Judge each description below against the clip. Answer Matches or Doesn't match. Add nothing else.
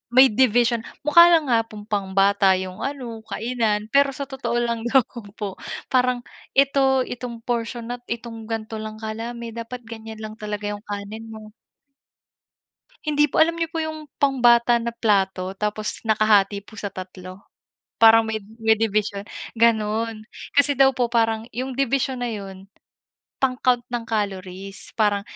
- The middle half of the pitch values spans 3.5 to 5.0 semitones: Doesn't match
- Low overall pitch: Doesn't match